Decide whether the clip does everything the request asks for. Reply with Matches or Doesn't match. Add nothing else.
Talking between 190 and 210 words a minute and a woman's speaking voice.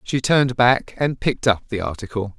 Doesn't match